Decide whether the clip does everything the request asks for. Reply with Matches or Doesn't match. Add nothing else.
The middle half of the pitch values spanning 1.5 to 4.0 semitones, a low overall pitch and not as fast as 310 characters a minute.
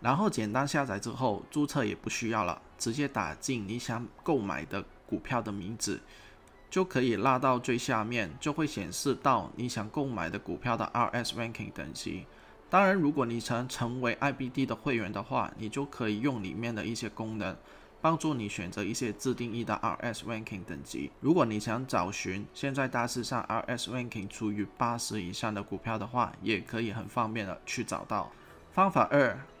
Doesn't match